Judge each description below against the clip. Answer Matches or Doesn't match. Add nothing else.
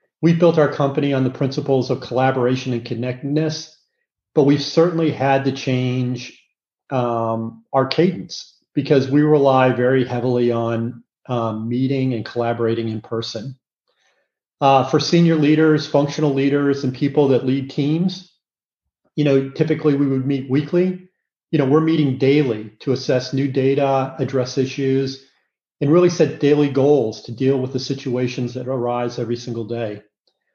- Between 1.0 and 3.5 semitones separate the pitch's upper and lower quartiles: Matches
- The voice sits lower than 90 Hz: Doesn't match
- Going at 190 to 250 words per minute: Doesn't match